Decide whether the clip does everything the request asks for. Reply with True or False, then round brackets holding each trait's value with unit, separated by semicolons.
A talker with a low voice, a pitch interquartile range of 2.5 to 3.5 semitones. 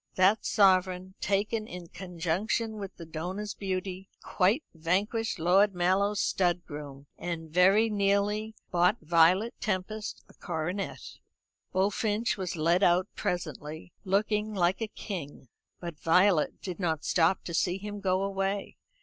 False (185 Hz; 2.8 semitones)